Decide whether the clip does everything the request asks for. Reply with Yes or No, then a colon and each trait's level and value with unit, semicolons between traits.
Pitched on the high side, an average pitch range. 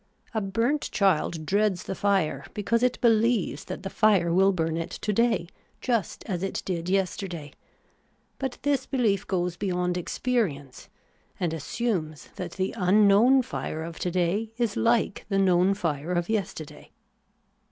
Yes: high, 195 Hz; average, 4.2 semitones